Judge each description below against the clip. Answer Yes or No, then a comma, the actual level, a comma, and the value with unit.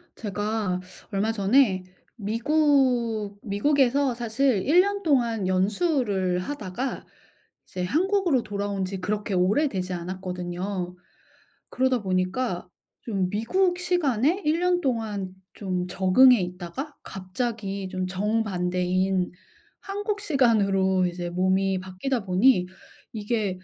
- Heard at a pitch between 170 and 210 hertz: Yes, high, 205 Hz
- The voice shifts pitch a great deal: Yes, wide, 5.9 semitones